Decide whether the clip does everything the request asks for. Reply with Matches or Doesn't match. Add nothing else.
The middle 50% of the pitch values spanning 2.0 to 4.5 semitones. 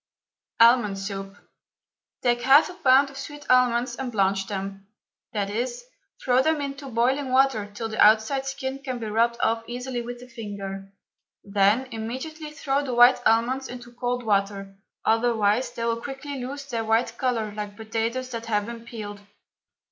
Matches